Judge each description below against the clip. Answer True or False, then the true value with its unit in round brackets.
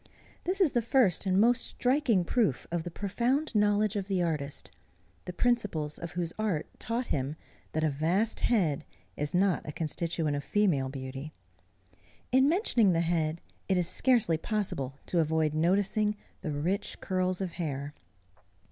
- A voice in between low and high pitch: True (180 Hz)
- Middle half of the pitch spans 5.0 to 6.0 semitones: True (5.5 semitones)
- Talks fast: False (155 wpm)